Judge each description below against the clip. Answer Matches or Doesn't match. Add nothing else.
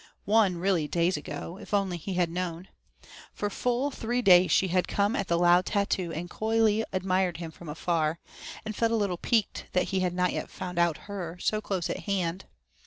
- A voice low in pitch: Doesn't match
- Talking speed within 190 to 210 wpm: Matches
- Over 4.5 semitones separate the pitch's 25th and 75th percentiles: Doesn't match